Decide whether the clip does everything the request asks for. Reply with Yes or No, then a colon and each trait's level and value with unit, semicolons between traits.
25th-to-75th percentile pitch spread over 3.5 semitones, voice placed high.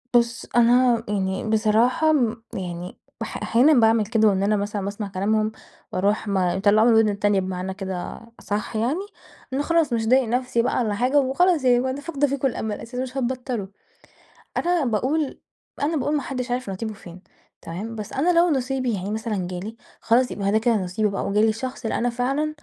Yes: average, 4.0 semitones; high, 230 Hz